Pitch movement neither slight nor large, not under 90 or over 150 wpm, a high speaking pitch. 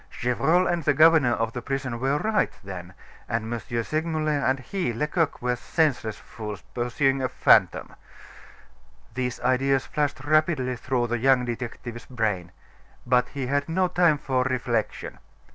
No: average, 3.8 semitones; average, 145 wpm; low, 130 Hz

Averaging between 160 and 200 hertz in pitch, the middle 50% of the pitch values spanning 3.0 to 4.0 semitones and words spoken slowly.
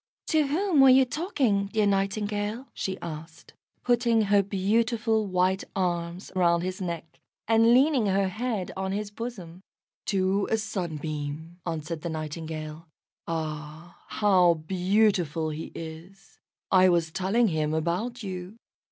No: high, 190 Hz; average, 4.6 semitones; slow, 130 wpm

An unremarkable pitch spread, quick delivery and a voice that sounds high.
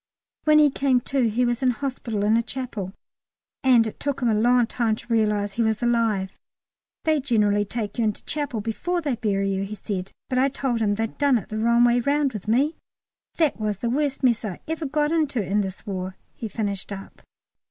Yes: average, 4.2 semitones; fast, 215 wpm; high, 230 Hz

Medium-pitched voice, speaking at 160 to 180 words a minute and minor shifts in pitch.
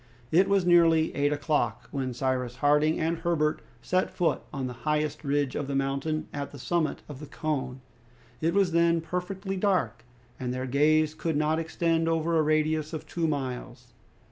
No: medium, 155 Hz; average, 175 wpm; average, 3.0 semitones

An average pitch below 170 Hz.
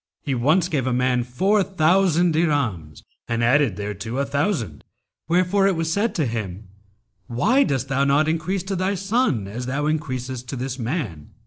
Yes: medium, 140 Hz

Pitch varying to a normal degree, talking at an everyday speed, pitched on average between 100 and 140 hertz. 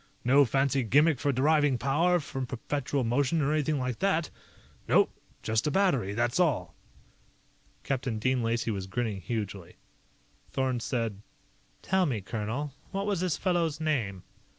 Yes: average, 4.9 semitones; average, 145 wpm; low, 135 Hz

